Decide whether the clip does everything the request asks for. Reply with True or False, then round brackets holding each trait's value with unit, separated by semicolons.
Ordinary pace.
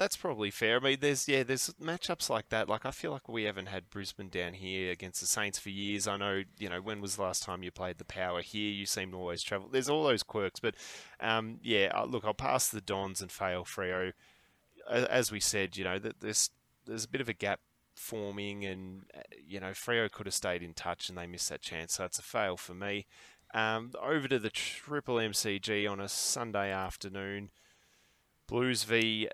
False (215 wpm)